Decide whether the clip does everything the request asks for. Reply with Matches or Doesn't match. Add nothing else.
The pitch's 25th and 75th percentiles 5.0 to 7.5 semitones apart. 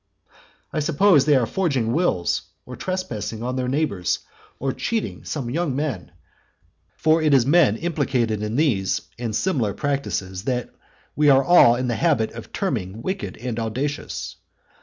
Matches